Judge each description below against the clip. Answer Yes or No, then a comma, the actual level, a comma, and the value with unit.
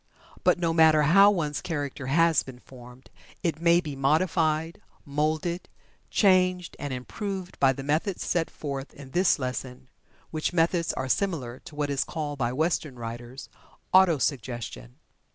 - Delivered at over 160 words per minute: No, average, 150 wpm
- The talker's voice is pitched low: No, medium, 150 Hz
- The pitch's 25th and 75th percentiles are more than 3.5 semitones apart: Yes, average, 4.2 semitones